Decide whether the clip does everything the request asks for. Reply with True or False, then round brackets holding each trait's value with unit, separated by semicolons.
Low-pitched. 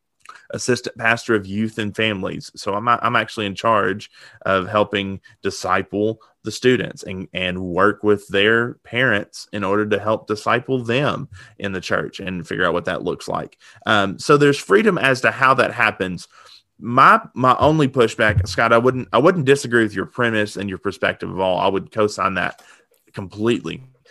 True (110 Hz)